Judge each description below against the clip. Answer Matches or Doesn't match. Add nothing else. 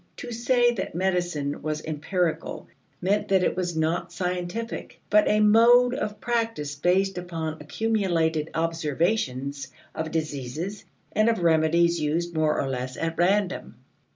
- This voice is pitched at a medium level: Matches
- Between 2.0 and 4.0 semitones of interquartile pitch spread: Doesn't match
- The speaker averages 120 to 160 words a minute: Matches